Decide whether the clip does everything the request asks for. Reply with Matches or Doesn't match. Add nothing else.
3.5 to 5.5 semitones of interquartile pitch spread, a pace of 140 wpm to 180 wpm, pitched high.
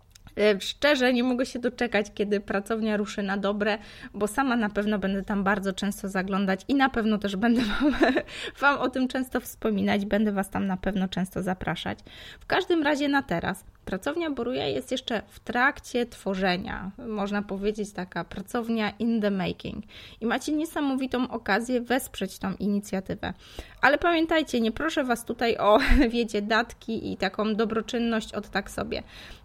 Matches